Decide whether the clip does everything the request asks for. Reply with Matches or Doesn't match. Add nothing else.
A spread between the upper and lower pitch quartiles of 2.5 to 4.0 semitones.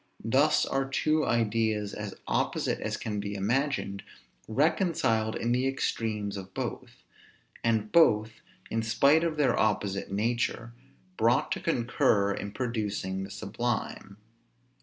Matches